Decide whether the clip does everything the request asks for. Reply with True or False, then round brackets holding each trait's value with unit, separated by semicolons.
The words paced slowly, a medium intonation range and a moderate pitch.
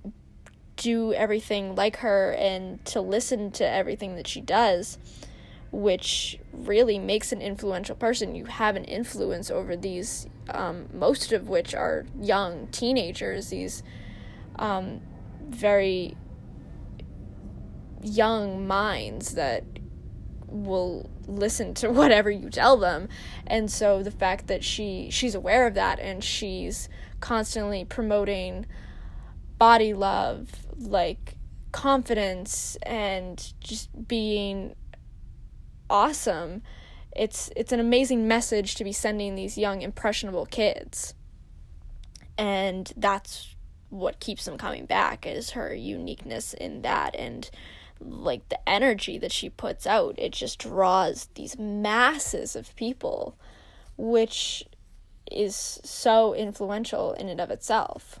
False (115 wpm; 3.1 semitones; 210 Hz)